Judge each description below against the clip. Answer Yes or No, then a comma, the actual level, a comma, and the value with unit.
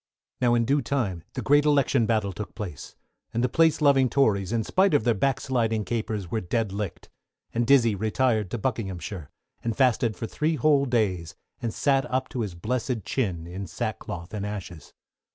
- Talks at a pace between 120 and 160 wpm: No, average, 185 wpm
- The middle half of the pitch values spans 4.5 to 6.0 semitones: Yes, average, 4.8 semitones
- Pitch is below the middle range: Yes, low, 115 Hz